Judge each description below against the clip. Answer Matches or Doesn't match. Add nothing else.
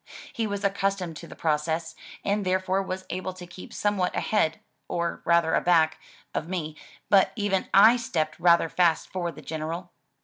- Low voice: Doesn't match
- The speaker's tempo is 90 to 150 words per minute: Doesn't match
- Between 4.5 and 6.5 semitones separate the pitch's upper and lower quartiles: Doesn't match